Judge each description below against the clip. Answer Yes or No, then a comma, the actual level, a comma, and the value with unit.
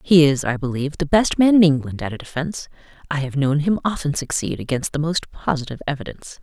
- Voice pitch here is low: No, medium, 150 Hz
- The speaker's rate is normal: No, fast, 215 wpm